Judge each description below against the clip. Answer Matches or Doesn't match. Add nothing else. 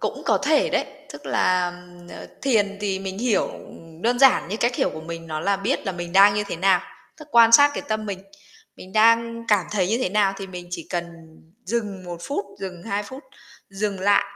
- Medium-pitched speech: Doesn't match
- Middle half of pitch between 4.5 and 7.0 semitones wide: Doesn't match